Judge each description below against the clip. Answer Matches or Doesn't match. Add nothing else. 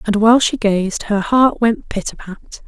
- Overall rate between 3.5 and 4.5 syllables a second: Matches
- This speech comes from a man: Doesn't match